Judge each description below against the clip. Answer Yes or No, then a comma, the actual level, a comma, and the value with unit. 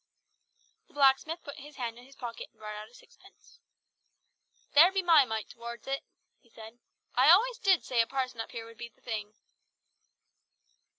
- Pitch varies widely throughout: No, average, 4.4 semitones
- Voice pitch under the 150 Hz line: No, very high, 250 Hz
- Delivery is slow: No, average, 175 wpm